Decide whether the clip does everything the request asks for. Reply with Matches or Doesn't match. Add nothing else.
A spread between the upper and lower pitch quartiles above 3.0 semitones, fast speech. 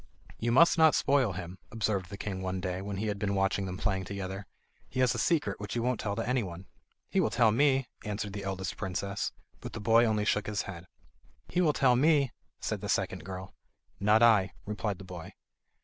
Matches